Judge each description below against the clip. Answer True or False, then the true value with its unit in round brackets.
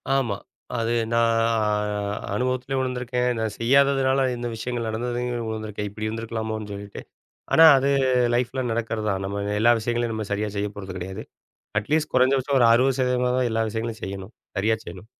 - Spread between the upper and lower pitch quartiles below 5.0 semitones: True (2.8 semitones)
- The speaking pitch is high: False (115 Hz)